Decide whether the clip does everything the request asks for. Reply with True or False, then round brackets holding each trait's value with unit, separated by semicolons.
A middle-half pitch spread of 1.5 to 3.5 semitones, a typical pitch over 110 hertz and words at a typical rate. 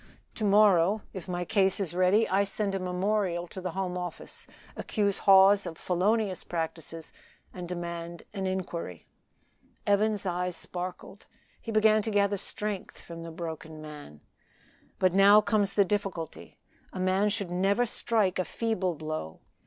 True (2.9 semitones; 185 Hz; 150 wpm)